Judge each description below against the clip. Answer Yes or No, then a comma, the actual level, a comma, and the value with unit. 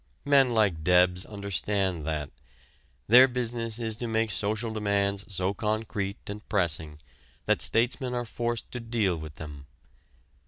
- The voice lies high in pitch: No, low, 105 Hz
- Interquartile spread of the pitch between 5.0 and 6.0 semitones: No, average, 4.2 semitones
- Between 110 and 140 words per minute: Yes, slow, 135 wpm